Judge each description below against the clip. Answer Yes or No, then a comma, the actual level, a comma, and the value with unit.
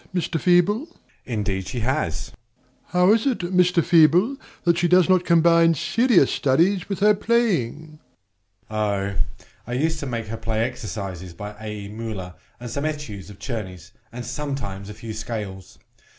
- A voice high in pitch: No, low, 130 Hz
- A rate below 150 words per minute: No, average, 165 wpm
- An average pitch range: No, wide, 8.9 semitones